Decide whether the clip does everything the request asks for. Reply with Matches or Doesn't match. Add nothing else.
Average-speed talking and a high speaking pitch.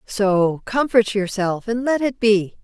Matches